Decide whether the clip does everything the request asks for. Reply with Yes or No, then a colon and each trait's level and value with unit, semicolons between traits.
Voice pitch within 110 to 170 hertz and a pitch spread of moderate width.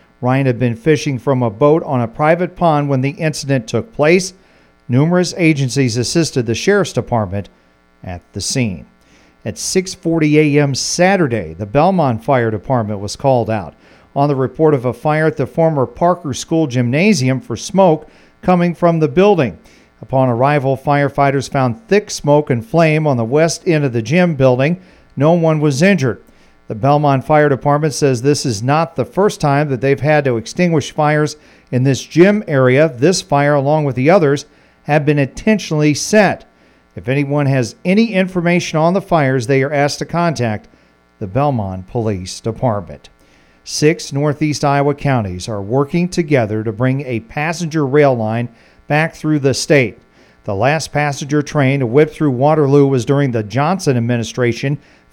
Yes: medium, 140 Hz; average, 4.3 semitones